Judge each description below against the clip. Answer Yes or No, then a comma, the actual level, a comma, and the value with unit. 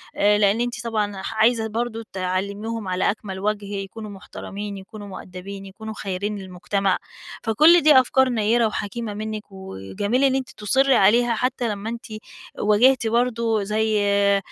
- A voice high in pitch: Yes, high, 210 Hz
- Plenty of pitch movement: No, average, 2.8 semitones